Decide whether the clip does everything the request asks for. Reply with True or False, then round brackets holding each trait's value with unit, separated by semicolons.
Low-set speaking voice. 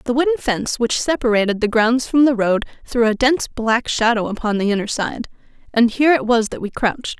False (235 Hz)